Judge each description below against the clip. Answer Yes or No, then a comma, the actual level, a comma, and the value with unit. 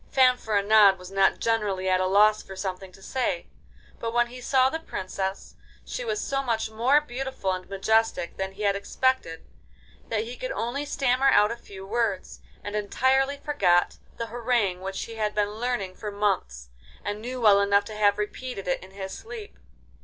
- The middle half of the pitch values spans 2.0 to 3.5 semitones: No, average, 4.4 semitones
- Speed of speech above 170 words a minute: Yes, average, 185 wpm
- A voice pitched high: Yes, high, 215 Hz